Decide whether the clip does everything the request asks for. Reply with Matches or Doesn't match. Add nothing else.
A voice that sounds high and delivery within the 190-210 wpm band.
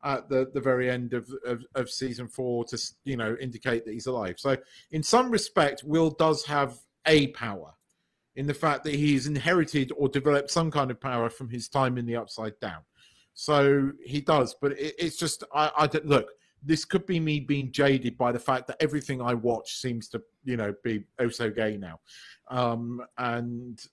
Doesn't match